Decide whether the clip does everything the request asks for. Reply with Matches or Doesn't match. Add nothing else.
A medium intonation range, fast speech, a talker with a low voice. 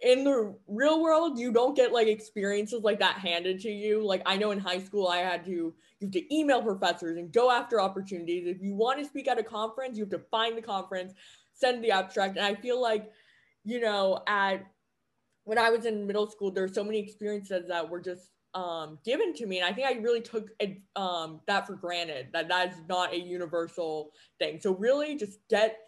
Doesn't match